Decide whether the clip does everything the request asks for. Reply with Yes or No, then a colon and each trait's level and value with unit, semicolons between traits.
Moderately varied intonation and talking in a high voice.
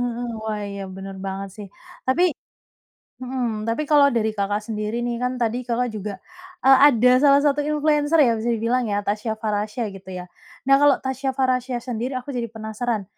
Yes: average, 3.5 semitones; high, 235 Hz